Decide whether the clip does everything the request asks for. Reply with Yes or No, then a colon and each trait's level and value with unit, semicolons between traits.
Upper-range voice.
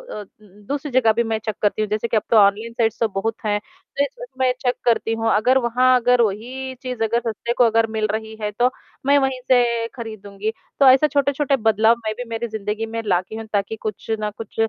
Yes: high, 225 Hz